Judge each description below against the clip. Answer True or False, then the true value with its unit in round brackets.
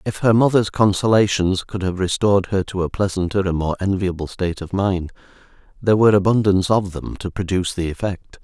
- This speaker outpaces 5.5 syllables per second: True (6.0 syllables/s)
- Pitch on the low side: True (95 Hz)